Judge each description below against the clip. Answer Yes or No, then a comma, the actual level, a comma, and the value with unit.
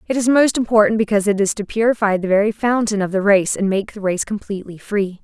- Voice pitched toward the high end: Yes, high, 205 Hz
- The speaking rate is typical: No, fast, 240 wpm